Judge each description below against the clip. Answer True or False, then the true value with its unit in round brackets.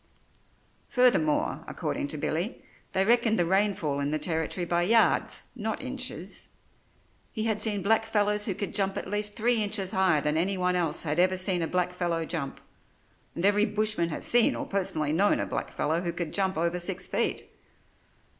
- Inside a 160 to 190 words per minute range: True (170 wpm)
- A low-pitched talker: False (185 Hz)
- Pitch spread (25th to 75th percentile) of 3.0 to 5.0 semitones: True (3.7 semitones)